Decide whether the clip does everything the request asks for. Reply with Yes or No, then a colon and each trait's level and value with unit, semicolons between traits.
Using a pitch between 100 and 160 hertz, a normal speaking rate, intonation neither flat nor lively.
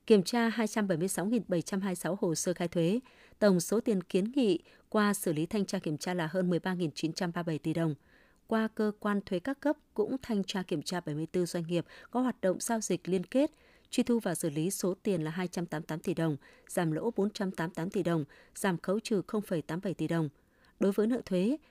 No: medium, 185 Hz; average, 195 wpm; average, 4.1 semitones